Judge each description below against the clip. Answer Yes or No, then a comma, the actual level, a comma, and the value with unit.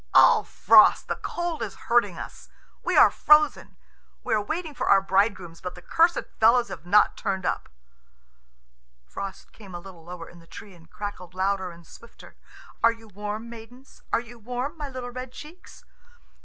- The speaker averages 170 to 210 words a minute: Yes, average, 175 wpm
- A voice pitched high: Yes, high, 210 Hz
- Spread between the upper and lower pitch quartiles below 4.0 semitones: No, average, 4.9 semitones